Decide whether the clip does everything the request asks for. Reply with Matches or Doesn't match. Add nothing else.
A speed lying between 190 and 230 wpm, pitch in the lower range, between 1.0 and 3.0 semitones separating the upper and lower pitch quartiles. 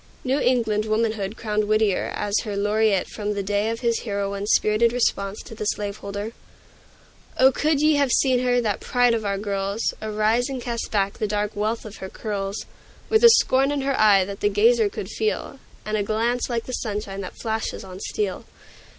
Doesn't match